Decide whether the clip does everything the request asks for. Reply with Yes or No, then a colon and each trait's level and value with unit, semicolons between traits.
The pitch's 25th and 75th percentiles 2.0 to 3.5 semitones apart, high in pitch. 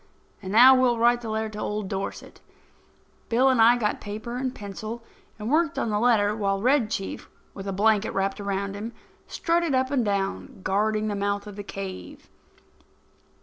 Yes: average, 3.1 semitones; high, 215 Hz